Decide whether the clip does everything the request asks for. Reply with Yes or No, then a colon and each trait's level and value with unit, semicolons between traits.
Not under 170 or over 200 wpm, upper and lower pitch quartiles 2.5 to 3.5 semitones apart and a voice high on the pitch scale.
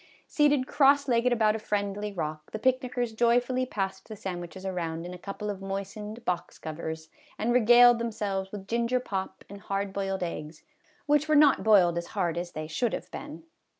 No: average, 185 wpm; average, 4.6 semitones; high, 205 Hz